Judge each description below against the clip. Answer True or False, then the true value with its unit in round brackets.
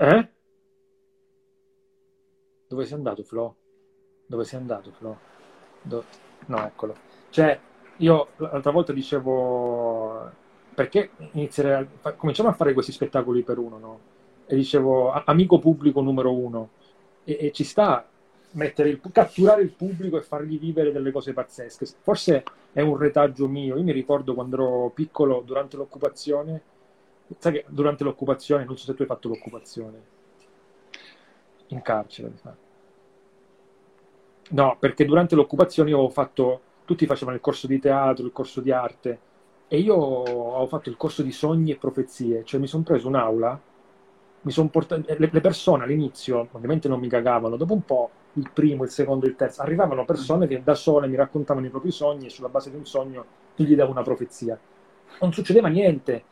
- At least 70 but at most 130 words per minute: False (160 wpm)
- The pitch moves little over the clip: False (3.8 semitones)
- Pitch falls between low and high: True (145 Hz)